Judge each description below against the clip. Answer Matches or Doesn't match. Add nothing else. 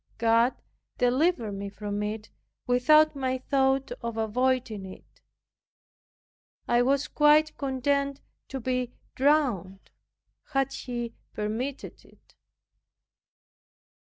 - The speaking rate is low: Matches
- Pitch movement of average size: Matches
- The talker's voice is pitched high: Matches